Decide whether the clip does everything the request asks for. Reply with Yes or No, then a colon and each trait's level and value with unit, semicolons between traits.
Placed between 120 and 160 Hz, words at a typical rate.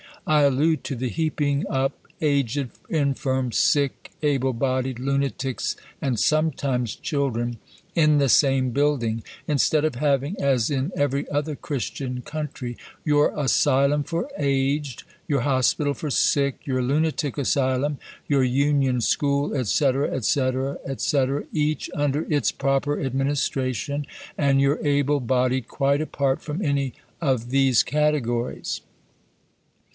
No: medium, 140 Hz; slow, 120 wpm